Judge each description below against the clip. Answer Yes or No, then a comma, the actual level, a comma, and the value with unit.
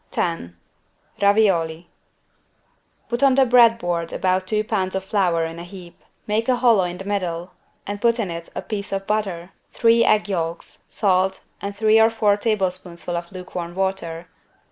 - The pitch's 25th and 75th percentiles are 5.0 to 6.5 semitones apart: No, average, 3.7 semitones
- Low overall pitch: No, high, 190 Hz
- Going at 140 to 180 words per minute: Yes, average, 165 wpm